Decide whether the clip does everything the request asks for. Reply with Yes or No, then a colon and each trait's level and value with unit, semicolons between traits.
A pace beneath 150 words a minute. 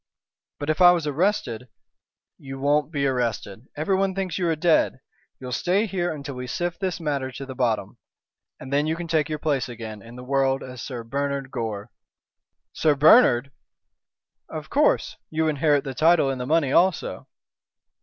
No: average, 175 wpm